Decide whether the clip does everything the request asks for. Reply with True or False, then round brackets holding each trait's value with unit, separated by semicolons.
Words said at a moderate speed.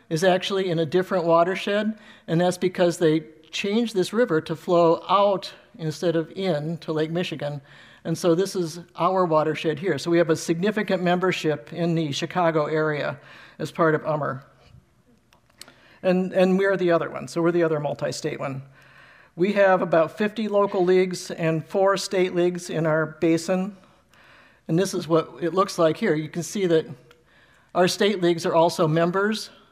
True (175 wpm)